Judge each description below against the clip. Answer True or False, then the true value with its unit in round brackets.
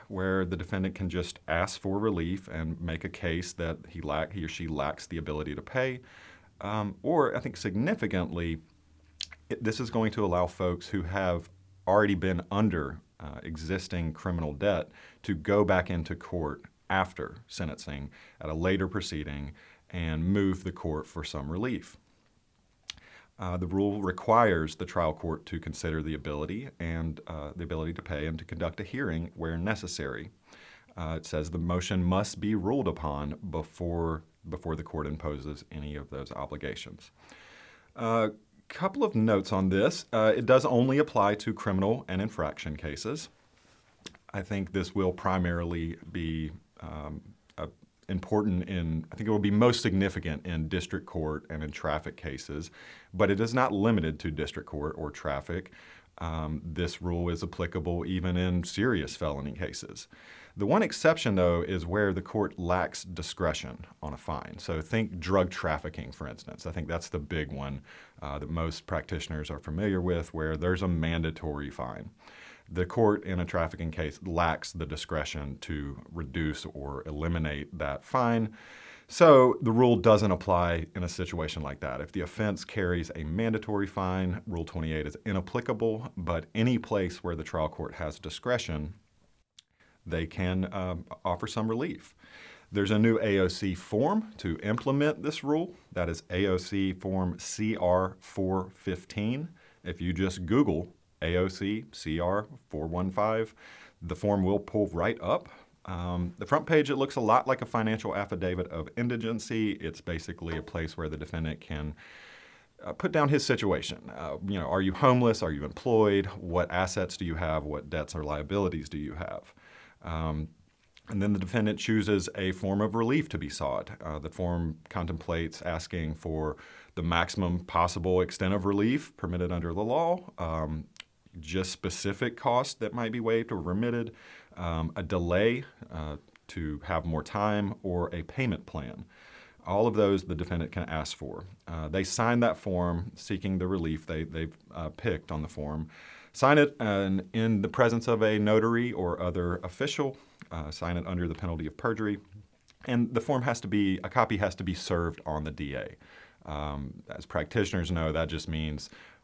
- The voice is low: True (90 Hz)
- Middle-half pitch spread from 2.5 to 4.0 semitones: False (4.4 semitones)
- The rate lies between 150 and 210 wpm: True (165 wpm)